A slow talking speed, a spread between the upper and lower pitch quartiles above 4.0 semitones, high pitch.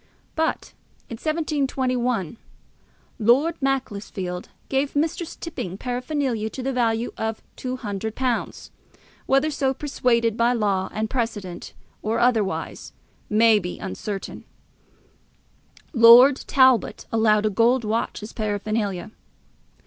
No: slow, 105 wpm; average, 3.7 semitones; high, 230 Hz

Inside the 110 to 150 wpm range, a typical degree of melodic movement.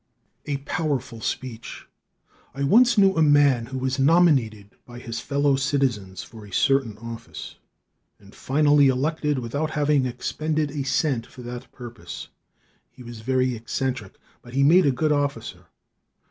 Yes: average, 145 wpm; average, 3.6 semitones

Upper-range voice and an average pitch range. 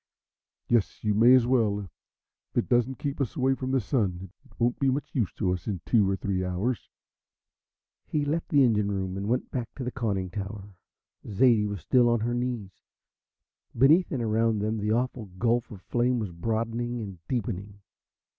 No: low, 115 Hz; average, 3.7 semitones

